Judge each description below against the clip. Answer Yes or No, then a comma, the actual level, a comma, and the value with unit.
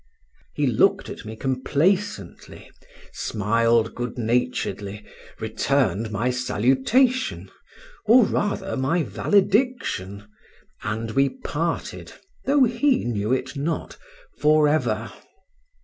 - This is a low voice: Yes, low, 130 Hz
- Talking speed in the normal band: No, slow, 95 wpm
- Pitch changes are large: Yes, wide, 8.6 semitones